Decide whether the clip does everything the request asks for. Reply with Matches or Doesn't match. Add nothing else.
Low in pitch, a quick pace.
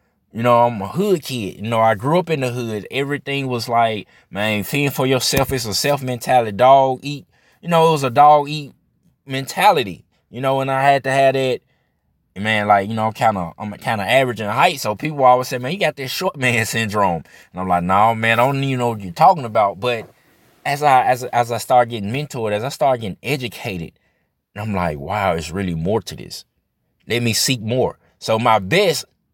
Matches